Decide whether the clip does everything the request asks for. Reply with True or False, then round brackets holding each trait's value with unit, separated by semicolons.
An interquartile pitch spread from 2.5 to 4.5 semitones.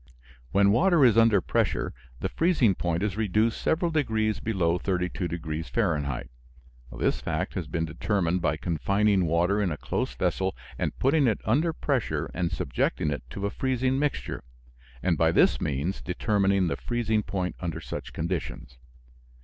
False (5.2 semitones)